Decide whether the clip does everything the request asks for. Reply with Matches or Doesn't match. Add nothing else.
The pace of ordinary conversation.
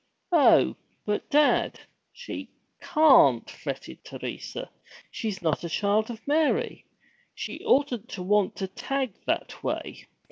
Doesn't match